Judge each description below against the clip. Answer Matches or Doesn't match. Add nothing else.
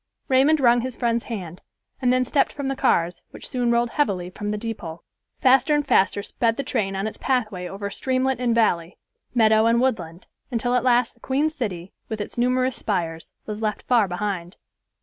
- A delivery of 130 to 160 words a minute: Doesn't match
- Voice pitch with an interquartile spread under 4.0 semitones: Doesn't match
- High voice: Matches